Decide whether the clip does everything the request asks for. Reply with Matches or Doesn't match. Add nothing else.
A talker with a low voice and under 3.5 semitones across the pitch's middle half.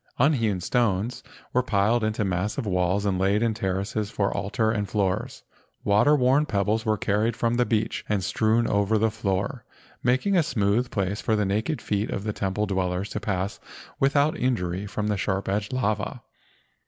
Matches